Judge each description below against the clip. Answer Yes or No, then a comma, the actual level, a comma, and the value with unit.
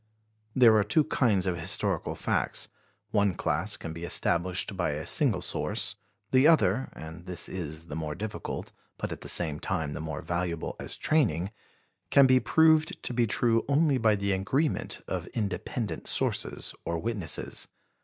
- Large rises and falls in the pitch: Yes, wide, 6.2 semitones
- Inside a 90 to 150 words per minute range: No, average, 165 wpm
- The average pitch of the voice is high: No, low, 100 Hz